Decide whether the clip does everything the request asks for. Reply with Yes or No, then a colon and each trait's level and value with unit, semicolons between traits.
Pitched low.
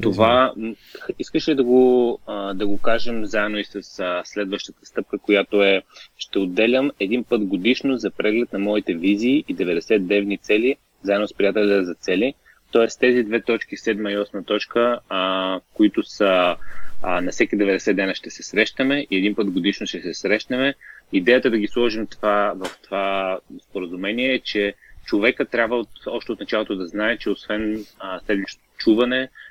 Yes: low, 110 Hz